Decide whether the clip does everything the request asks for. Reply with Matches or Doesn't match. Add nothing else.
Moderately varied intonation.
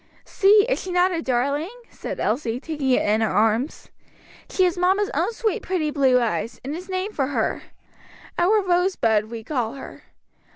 Doesn't match